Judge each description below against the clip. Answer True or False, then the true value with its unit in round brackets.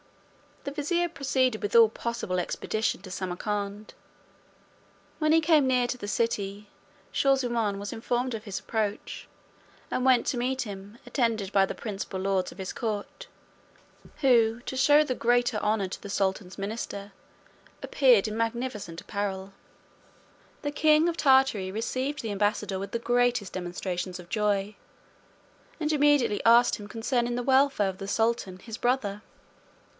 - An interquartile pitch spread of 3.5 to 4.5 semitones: True (4.2 semitones)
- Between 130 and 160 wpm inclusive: True (150 wpm)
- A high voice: True (225 Hz)